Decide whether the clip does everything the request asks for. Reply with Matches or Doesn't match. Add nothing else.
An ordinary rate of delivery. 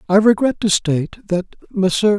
Matches